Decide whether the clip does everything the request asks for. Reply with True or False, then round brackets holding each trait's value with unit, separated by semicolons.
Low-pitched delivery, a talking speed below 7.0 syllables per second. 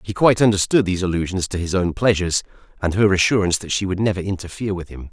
False (95 Hz; 7.3 syllables/s)